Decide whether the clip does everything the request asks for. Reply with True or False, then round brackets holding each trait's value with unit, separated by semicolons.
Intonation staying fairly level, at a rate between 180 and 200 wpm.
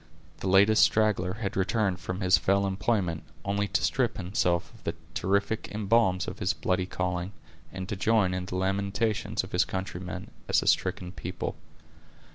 False (2.0 semitones; 165 wpm)